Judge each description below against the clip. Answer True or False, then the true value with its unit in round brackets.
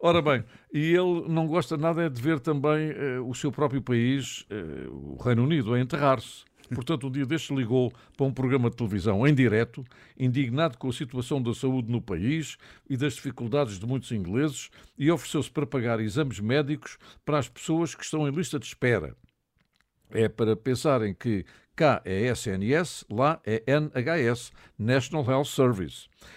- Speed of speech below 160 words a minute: False (170 wpm)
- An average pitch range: True (4.1 semitones)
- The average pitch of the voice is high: False (135 Hz)